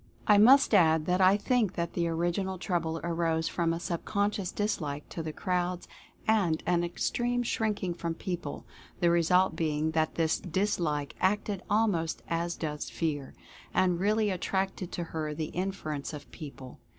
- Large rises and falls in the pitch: No, average, 3.2 semitones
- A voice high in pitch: No, medium, 175 Hz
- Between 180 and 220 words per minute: No, average, 160 wpm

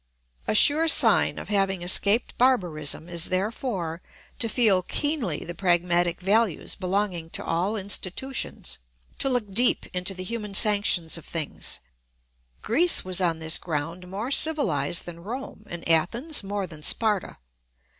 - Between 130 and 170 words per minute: Yes, average, 140 wpm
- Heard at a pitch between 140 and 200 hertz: Yes, high, 190 Hz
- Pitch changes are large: No, average, 4.7 semitones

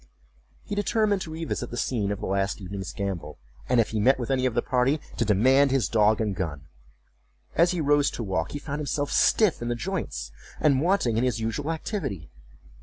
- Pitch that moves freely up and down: Yes, wide, 6.3 semitones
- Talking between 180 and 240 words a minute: Yes, fast, 205 wpm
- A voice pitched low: Yes, low, 125 Hz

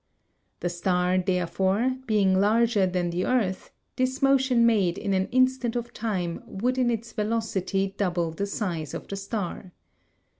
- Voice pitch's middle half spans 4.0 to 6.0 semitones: Yes, average, 4.3 semitones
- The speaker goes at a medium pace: Yes, average, 150 wpm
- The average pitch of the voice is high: Yes, high, 200 Hz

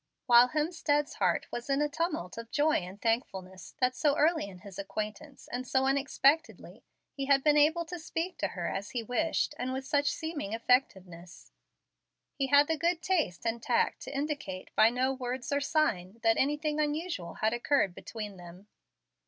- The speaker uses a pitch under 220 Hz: No, very high, 265 Hz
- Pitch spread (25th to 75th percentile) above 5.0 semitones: Yes, wide, 5.6 semitones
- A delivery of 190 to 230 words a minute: No, average, 175 wpm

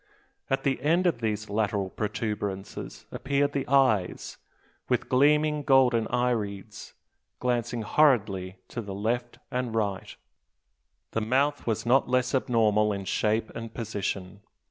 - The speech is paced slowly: Yes, slow, 125 wpm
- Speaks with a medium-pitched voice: No, low, 115 Hz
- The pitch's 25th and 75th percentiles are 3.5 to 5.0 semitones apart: Yes, average, 4.1 semitones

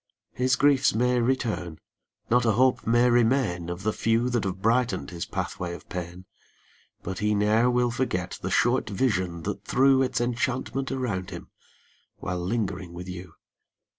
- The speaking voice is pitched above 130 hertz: No, low, 115 Hz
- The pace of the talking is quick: No, average, 165 wpm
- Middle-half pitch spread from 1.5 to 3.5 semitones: No, wide, 5.5 semitones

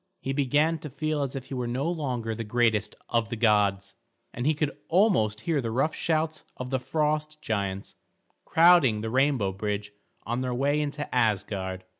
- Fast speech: No, average, 180 wpm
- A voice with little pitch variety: No, wide, 5.5 semitones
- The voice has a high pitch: No, low, 125 Hz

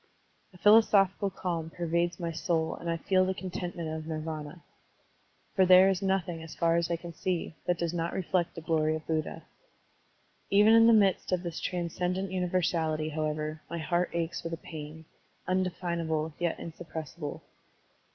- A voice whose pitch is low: No, medium, 170 Hz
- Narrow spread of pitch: Yes, narrow, 2.3 semitones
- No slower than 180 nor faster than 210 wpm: No, average, 160 wpm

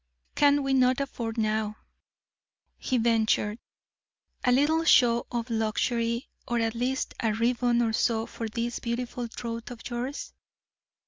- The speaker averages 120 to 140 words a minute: Yes, slow, 135 wpm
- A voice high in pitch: Yes, high, 235 Hz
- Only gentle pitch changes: Yes, narrow, 1.9 semitones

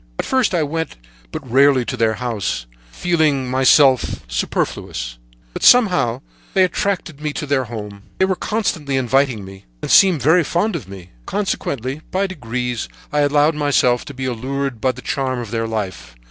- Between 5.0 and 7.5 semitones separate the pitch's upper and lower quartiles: Yes, average, 5.3 semitones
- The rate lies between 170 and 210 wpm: Yes, average, 175 wpm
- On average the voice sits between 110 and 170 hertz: Yes, low, 135 Hz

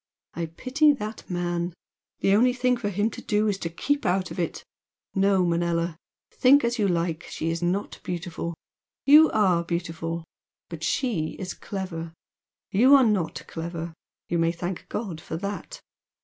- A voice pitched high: No, medium, 180 Hz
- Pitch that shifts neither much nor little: Yes, average, 4.2 semitones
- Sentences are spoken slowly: No, average, 165 wpm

